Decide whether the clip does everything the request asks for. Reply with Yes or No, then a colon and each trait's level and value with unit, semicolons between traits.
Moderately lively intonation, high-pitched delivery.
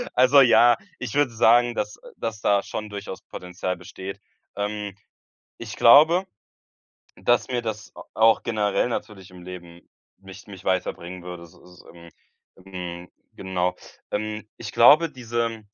No: average, 4.2 semitones; low, 105 Hz